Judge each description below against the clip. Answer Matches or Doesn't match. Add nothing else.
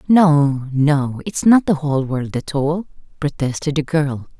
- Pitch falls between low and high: Matches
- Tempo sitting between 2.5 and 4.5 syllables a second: Matches